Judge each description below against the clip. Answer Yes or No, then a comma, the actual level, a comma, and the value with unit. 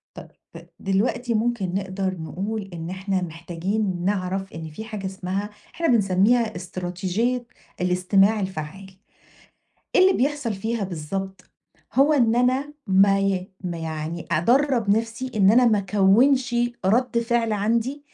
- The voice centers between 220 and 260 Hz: No, high, 195 Hz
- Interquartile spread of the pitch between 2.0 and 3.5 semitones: No, average, 4.2 semitones